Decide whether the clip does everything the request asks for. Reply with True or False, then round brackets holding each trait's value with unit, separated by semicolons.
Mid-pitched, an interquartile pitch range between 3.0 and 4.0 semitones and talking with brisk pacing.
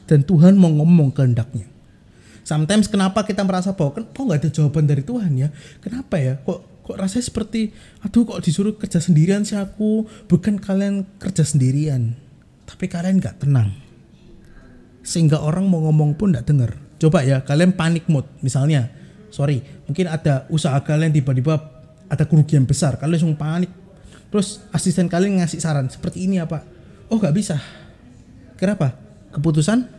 False (165 Hz; 4.9 semitones; 155 wpm)